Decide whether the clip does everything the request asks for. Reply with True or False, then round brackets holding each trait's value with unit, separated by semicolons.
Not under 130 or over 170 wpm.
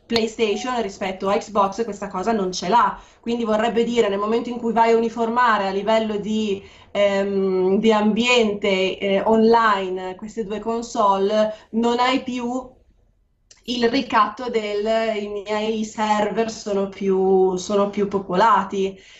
True (140 wpm)